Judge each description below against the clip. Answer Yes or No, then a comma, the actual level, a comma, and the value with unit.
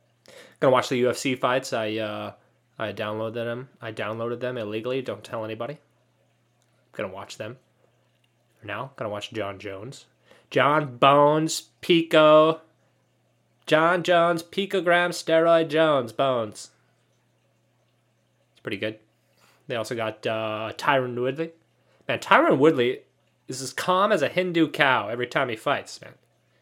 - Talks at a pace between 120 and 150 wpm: Yes, average, 140 wpm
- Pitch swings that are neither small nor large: No, wide, 6.3 semitones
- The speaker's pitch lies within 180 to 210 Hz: No, low, 125 Hz